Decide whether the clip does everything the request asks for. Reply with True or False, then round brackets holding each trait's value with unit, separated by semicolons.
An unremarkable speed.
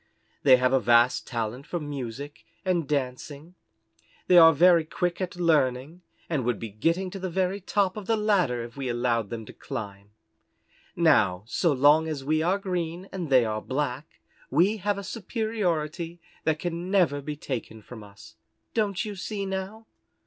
True (170 wpm)